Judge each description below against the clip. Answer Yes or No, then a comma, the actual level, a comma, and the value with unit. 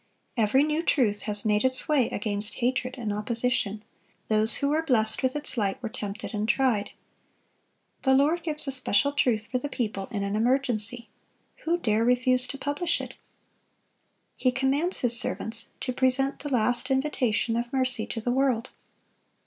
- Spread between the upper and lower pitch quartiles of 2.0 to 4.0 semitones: Yes, average, 3.7 semitones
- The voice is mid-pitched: No, very high, 250 Hz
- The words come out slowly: No, average, 165 wpm